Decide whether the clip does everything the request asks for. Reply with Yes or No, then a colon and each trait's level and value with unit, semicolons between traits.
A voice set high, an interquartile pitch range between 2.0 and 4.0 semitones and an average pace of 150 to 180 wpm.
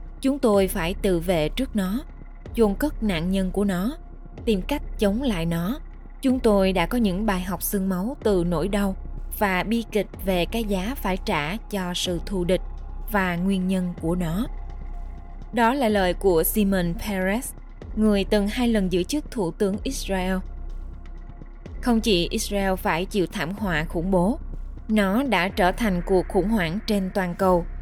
Yes: high, 195 Hz; average, 3.3 semitones; average, 175 wpm